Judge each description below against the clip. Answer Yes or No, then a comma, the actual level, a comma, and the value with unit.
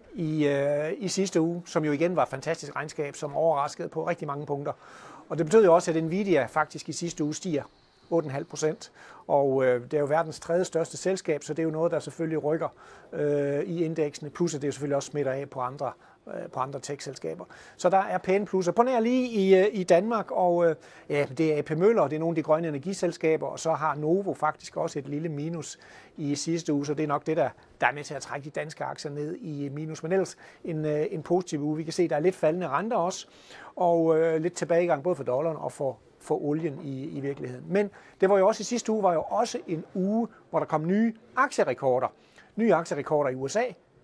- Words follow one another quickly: Yes, fast, 230 wpm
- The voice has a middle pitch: Yes, medium, 160 Hz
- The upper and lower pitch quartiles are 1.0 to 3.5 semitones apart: Yes, average, 3.1 semitones